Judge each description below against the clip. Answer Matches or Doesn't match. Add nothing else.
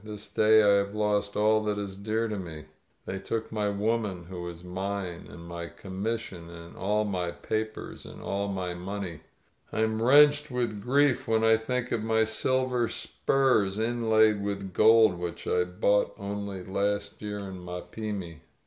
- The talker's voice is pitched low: Matches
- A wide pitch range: Doesn't match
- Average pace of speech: Matches